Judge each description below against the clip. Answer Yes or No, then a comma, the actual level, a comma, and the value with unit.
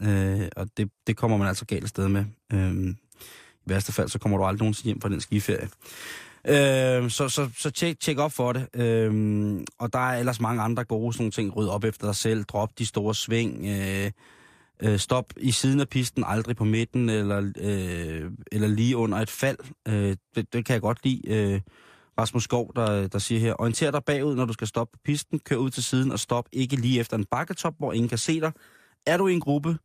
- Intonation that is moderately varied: Yes, average, 3.7 semitones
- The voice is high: No, low, 115 Hz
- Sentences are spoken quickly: Yes, fast, 230 wpm